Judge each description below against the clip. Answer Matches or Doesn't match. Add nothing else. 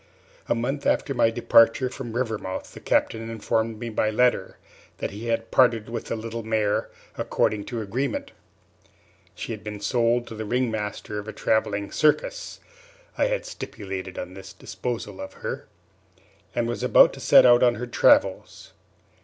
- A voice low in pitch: Matches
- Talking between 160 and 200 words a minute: Matches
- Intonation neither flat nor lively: Doesn't match